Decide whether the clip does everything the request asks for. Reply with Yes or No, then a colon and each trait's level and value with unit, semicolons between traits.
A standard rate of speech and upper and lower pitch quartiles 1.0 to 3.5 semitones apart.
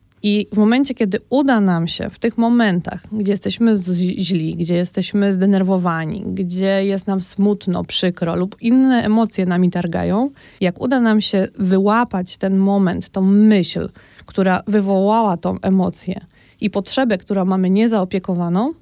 Yes: average, 145 wpm; narrow, 2.6 semitones